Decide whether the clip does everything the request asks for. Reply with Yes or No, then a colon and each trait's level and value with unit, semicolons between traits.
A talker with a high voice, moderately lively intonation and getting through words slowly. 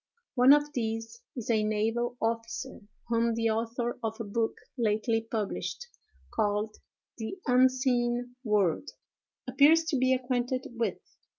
No: high, 235 Hz; narrow, 2.3 semitones; slow, 125 wpm